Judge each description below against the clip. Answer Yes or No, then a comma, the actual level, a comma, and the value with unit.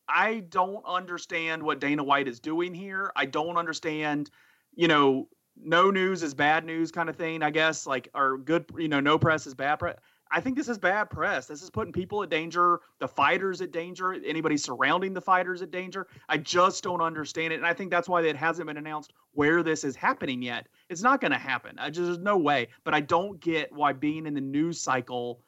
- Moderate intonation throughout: Yes, average, 3.3 semitones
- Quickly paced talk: Yes, fast, 225 wpm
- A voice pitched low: No, medium, 165 Hz